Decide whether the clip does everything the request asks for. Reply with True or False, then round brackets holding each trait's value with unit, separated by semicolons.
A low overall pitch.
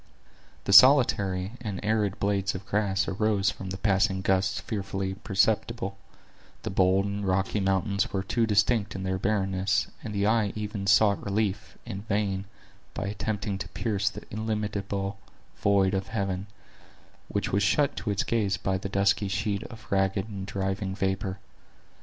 True (100 Hz)